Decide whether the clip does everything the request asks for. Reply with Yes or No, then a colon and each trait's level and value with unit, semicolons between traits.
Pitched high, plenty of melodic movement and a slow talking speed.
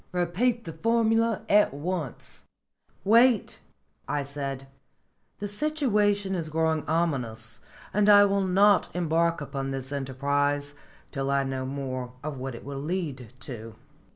No: medium, 160 Hz; wide, 6.8 semitones; slow, 130 wpm